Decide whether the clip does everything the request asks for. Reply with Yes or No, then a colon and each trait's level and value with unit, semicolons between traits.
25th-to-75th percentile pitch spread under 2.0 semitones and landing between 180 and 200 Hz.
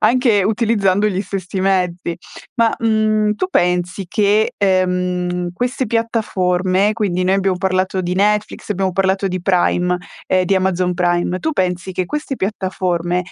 No: average, 2.7 semitones; high, 190 Hz